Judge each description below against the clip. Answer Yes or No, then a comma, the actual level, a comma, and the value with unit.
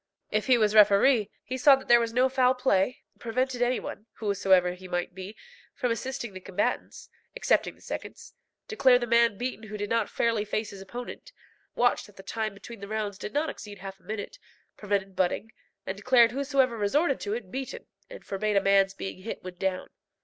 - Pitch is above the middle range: Yes, high, 215 Hz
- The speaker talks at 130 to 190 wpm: No, average, 200 wpm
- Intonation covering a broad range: No, average, 4.0 semitones